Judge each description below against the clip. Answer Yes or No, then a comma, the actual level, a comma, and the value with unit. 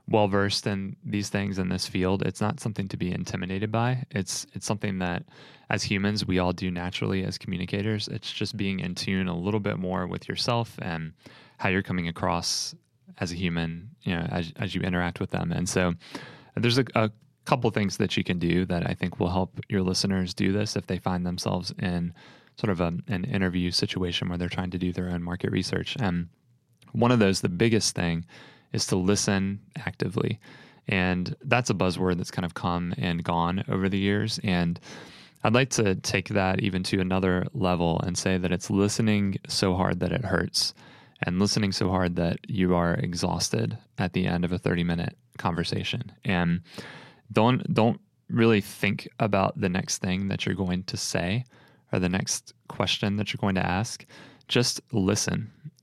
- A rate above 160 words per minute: Yes, average, 195 wpm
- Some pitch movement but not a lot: Yes, average, 3.0 semitones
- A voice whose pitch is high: No, very low, 95 Hz